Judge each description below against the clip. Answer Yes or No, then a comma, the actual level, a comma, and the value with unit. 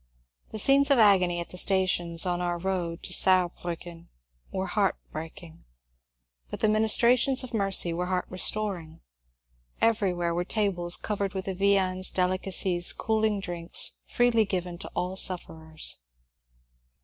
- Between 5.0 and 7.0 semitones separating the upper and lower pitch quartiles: No, average, 2.7 semitones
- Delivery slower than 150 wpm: Yes, average, 140 wpm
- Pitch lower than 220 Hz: Yes, medium, 185 Hz